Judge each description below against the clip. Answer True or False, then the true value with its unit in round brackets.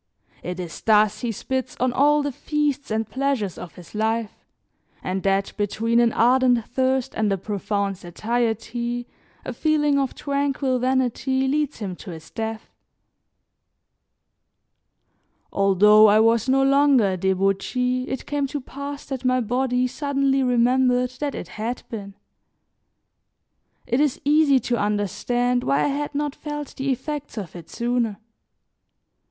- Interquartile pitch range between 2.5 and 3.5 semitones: False (4.3 semitones)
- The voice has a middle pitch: False (245 Hz)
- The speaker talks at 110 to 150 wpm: True (140 wpm)